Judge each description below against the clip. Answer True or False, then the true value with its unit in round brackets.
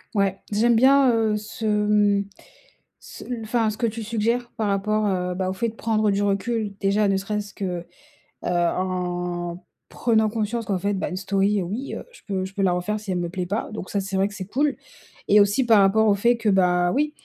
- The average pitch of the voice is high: True (205 Hz)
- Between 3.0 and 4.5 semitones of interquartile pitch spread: False (2.5 semitones)